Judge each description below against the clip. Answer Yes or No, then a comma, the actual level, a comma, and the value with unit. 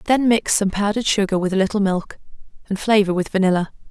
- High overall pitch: Yes, high, 200 Hz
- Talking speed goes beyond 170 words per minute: Yes, average, 200 wpm